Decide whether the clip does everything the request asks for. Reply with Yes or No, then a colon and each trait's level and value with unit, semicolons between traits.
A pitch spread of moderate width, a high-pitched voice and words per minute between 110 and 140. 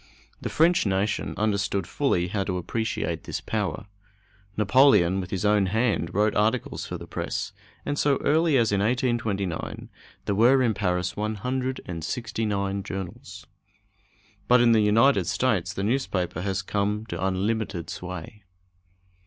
No: average, 3.7 semitones; low, 105 Hz; slow, 135 wpm